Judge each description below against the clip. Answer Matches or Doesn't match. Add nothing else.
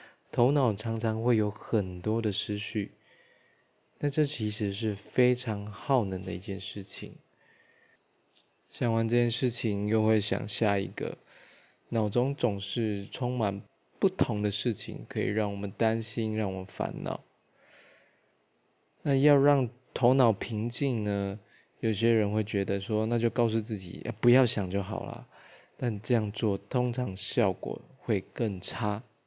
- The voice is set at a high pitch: Doesn't match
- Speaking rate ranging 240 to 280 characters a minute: Doesn't match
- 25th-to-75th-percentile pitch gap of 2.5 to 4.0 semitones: Matches